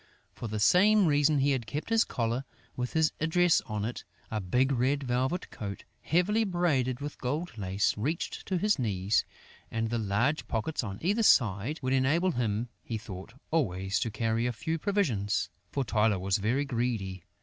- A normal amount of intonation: No, wide, 6.4 semitones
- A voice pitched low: Yes, low, 125 Hz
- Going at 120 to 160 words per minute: No, average, 175 wpm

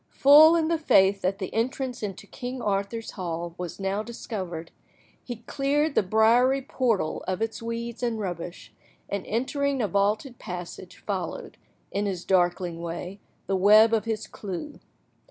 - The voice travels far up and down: No, average, 4.7 semitones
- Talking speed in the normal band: Yes, average, 155 wpm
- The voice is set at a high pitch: Yes, high, 210 Hz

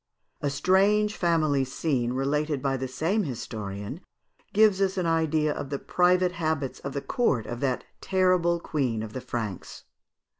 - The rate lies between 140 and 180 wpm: Yes, average, 155 wpm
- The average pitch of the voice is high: No, medium, 150 Hz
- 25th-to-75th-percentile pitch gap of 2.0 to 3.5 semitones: No, wide, 5.5 semitones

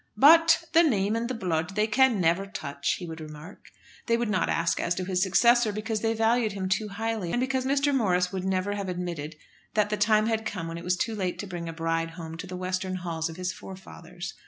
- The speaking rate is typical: No, fast, 235 wpm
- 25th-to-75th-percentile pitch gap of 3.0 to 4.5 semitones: Yes, average, 4.2 semitones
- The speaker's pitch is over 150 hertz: Yes, high, 190 Hz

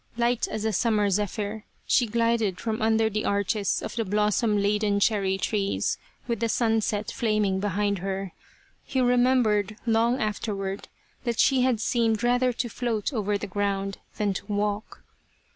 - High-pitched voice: Yes, high, 215 Hz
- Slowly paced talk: No, average, 155 wpm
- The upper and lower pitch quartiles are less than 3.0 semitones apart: Yes, narrow, 2.4 semitones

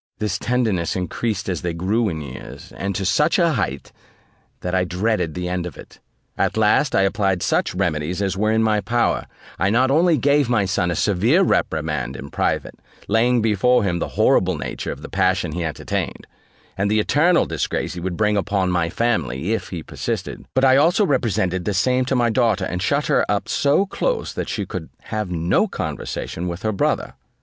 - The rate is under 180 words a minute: No, average, 195 wpm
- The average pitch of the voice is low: Yes, low, 100 Hz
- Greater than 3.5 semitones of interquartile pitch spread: Yes, average, 5.1 semitones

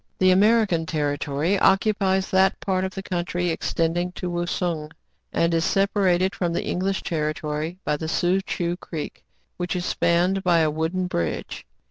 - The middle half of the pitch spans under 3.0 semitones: Yes, narrow, 2.6 semitones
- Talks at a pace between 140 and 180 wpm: Yes, average, 160 wpm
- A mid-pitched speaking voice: Yes, medium, 175 Hz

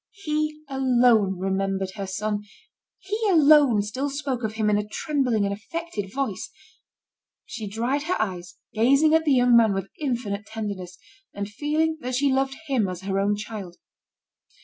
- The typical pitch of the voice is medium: No, high, 225 Hz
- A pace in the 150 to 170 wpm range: Yes, average, 160 wpm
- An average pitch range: No, wide, 5.8 semitones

